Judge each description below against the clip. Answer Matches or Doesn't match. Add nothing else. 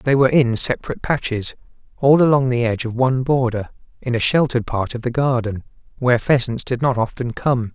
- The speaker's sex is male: Matches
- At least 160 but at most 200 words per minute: Matches